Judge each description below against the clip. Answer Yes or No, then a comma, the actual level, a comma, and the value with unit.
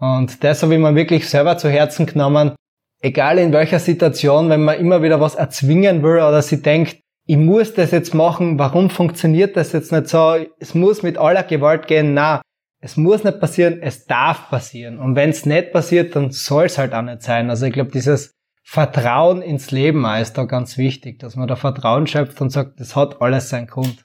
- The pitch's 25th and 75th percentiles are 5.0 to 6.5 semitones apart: No, average, 3.4 semitones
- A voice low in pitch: No, medium, 150 Hz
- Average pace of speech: No, fast, 210 wpm